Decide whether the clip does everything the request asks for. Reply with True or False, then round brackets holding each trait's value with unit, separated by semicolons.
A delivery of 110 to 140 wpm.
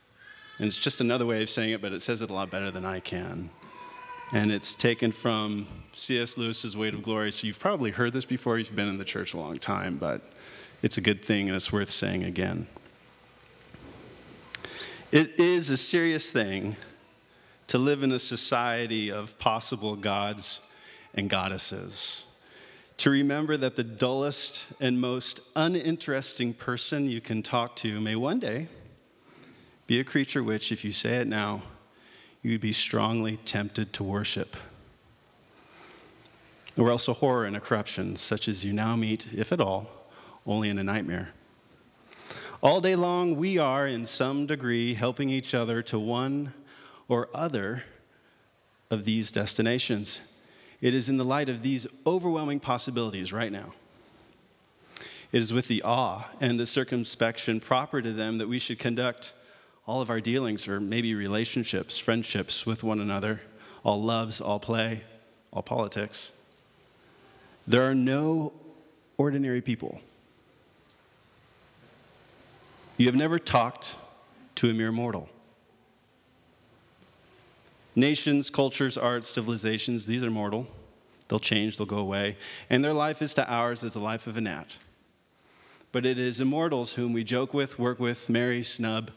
False (155 wpm)